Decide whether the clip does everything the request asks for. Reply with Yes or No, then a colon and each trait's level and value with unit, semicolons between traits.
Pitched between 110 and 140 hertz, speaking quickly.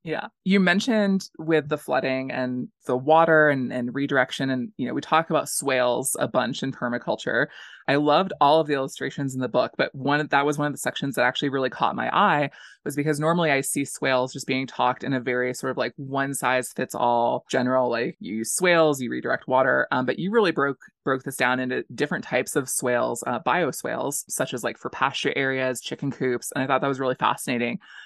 Yes: low, 135 Hz; fast, 220 wpm